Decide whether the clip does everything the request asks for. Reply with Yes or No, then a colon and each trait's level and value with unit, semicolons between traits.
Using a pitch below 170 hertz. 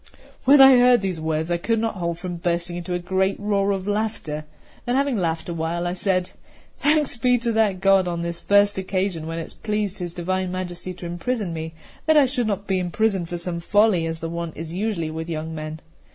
No: medium, 185 Hz